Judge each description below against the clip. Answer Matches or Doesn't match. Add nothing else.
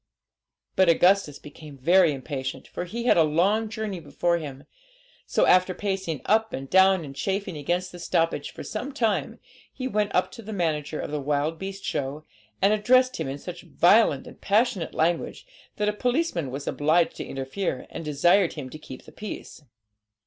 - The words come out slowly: Doesn't match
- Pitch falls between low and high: Matches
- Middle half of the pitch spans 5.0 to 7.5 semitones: Matches